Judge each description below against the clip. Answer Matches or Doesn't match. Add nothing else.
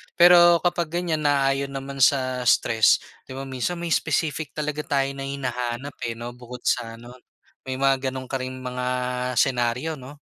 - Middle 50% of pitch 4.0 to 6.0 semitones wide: Doesn't match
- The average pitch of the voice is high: Doesn't match